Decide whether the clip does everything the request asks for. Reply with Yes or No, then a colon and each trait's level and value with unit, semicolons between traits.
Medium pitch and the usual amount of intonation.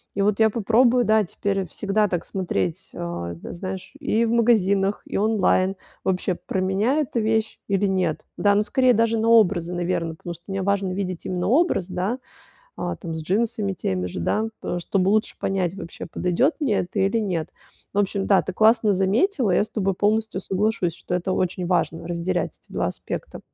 No: high, 195 Hz; average, 3.4 semitones